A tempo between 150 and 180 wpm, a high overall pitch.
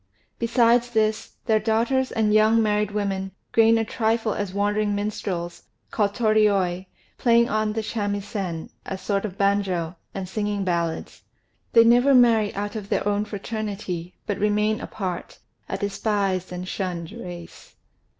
No: average, 140 wpm; high, 205 Hz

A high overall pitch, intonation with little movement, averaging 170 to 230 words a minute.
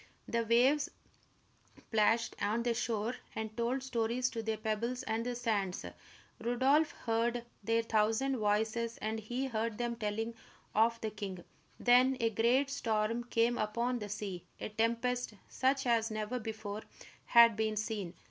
No: high, 230 Hz; narrow, 1.9 semitones; average, 150 wpm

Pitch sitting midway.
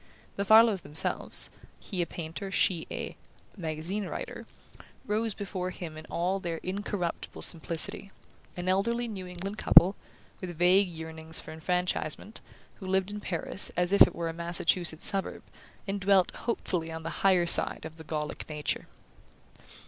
Yes: medium, 180 Hz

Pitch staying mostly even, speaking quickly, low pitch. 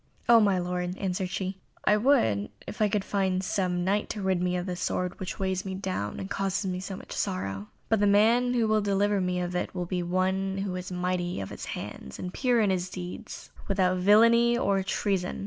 No: narrow, 2.1 semitones; fast, 210 wpm; high, 190 Hz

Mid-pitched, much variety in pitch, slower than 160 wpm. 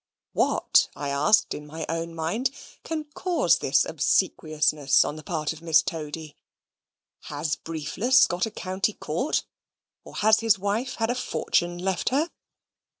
Yes: medium, 170 Hz; wide, 6.2 semitones; average, 150 wpm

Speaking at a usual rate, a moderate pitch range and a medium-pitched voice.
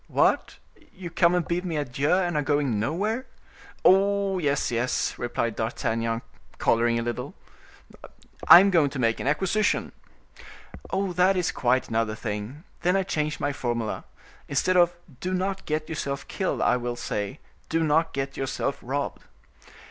No: average, 150 wpm; wide, 6.9 semitones; medium, 150 Hz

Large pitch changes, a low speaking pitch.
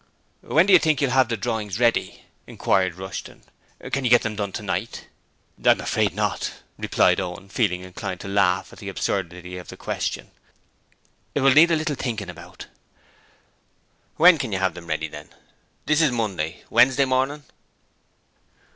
Yes: wide, 6.3 semitones; low, 110 Hz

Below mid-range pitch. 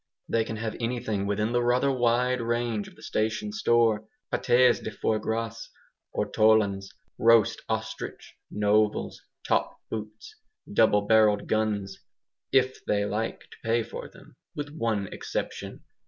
Yes: low, 110 Hz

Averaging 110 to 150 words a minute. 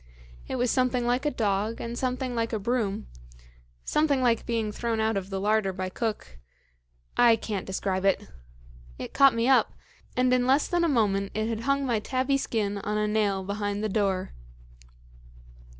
No: average, 180 wpm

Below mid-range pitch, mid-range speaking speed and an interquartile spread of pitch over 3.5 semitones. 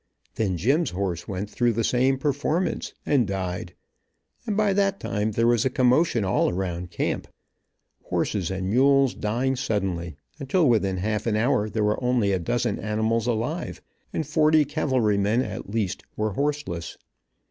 Yes: low, 115 Hz; average, 155 wpm; average, 5.2 semitones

